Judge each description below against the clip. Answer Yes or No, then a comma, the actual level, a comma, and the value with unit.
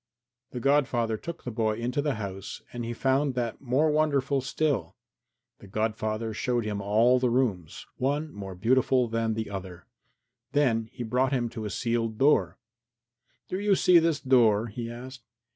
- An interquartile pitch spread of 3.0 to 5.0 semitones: Yes, average, 3.5 semitones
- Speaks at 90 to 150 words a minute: No, average, 165 wpm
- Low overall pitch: Yes, low, 120 Hz